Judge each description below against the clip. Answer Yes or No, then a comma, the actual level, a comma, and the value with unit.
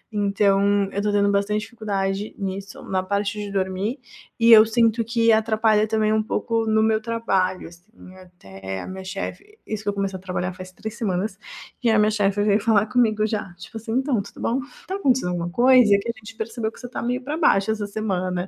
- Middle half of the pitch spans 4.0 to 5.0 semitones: No, narrow, 2.6 semitones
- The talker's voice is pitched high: Yes, high, 210 Hz